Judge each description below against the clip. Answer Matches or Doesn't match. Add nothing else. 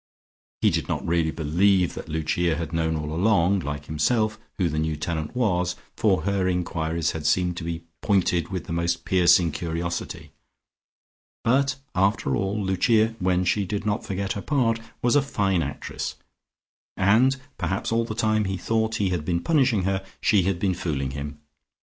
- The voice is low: Matches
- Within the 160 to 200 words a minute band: Matches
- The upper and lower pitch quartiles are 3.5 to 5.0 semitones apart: Matches